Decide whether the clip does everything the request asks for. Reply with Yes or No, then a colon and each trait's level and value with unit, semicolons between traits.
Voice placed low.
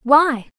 No: very high, 275 Hz